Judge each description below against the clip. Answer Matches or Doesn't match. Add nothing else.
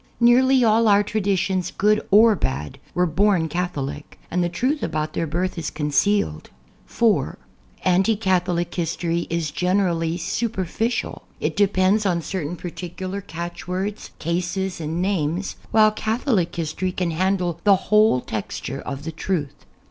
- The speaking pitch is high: Doesn't match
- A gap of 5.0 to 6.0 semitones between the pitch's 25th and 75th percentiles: Doesn't match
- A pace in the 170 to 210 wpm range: Doesn't match